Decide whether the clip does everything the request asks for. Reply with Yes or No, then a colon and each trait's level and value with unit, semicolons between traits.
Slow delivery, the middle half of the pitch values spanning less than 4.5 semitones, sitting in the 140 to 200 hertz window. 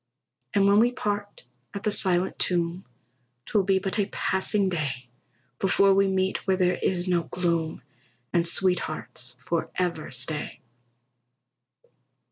Yes: slow, 125 wpm; average, 2.8 semitones; medium, 185 Hz